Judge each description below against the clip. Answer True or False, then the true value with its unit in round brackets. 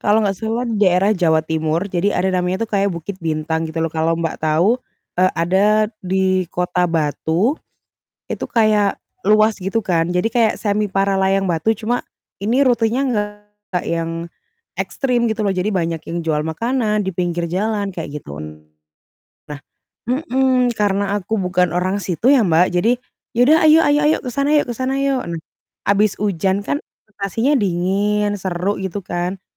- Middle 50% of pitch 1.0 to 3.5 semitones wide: False (3.9 semitones)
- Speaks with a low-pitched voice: False (195 Hz)